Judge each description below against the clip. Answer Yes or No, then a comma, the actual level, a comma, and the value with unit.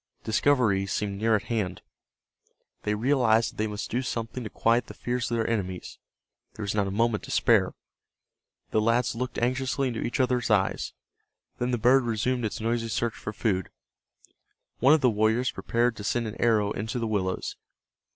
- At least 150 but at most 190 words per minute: Yes, average, 180 wpm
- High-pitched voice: No, low, 115 Hz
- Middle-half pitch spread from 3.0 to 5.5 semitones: No, narrow, 2.6 semitones